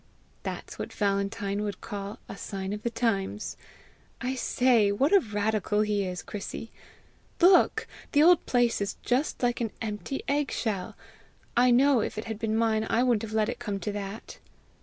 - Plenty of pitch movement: No, average, 3.1 semitones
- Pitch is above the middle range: Yes, high, 220 Hz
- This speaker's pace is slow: No, average, 180 wpm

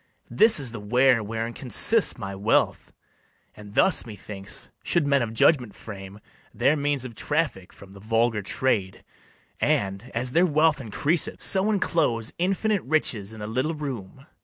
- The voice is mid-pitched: No, low, 120 Hz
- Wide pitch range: Yes, wide, 6.3 semitones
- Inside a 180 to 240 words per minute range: No, average, 155 wpm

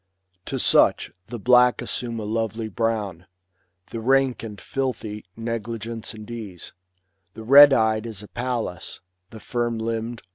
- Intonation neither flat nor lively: No, narrow, 1.6 semitones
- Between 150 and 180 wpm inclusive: No, average, 140 wpm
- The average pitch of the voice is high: No, low, 115 Hz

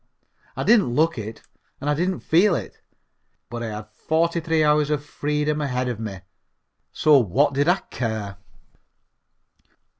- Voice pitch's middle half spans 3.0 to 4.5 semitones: No, average, 5.3 semitones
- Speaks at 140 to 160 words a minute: Yes, average, 150 wpm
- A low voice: No, medium, 145 Hz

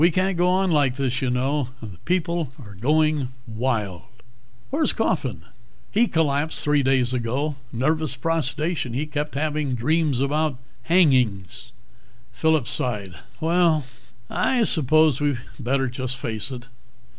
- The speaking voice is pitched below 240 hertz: Yes, medium, 140 Hz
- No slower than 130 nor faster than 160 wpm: Yes, slow, 135 wpm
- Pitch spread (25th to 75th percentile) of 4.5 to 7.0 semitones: No, average, 4.1 semitones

